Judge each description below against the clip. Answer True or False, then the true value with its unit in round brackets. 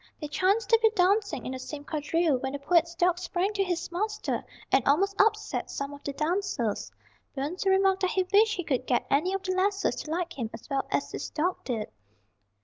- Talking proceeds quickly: True (215 wpm)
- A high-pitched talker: True (355 Hz)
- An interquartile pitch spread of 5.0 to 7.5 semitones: True (5.3 semitones)